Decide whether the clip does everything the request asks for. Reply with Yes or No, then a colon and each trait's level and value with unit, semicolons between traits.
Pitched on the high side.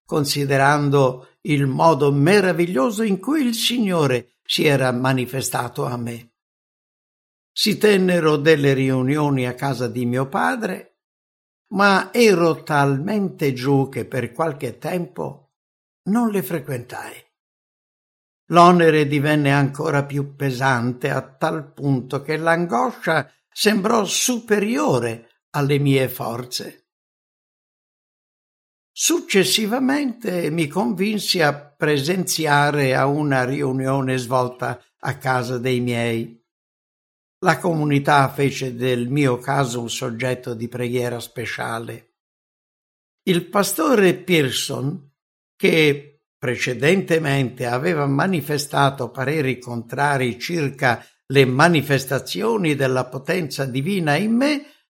No: medium, 140 Hz